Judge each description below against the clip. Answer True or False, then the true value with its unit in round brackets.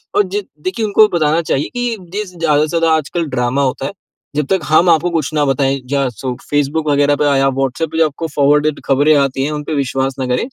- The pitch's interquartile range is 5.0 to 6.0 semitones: False (3.3 semitones)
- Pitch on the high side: False (150 Hz)